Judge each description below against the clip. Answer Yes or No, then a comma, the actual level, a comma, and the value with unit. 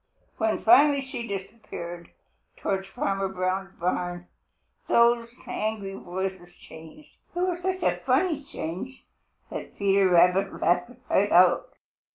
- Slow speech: Yes, slow, 120 wpm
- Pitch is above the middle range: Yes, high, 195 Hz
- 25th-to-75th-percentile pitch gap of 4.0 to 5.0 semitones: Yes, average, 4.6 semitones